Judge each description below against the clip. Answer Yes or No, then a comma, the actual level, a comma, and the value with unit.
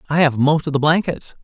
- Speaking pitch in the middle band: Yes, medium, 150 Hz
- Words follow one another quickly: Yes, fast, 250 wpm